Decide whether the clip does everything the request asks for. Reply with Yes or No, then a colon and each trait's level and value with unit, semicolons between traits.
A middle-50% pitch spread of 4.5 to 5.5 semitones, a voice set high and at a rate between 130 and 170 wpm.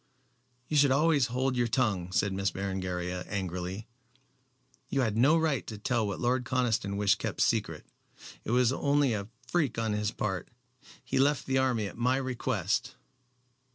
No: average, 4.8 semitones; low, 120 Hz; average, 160 wpm